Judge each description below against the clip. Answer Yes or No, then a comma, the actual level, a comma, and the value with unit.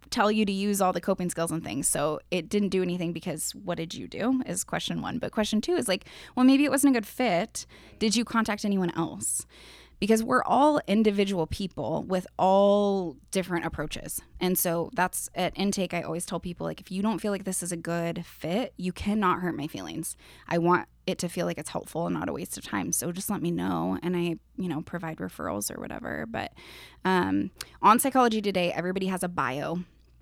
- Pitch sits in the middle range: Yes, medium, 180 Hz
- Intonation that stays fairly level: No, average, 3.5 semitones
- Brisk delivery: Yes, fast, 220 wpm